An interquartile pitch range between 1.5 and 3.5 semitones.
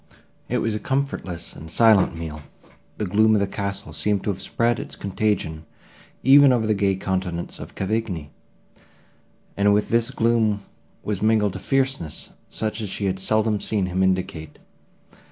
Yes: average, 2.9 semitones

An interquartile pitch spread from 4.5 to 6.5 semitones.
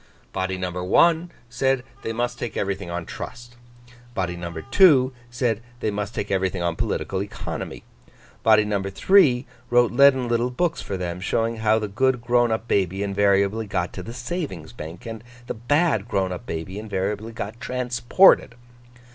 No: average, 4.1 semitones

